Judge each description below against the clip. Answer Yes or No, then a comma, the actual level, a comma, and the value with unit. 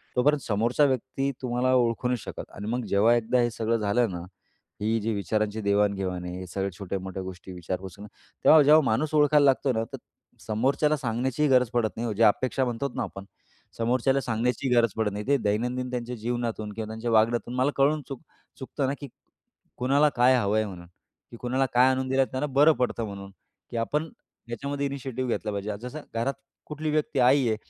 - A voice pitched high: No, low, 120 Hz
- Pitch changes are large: No, average, 3.8 semitones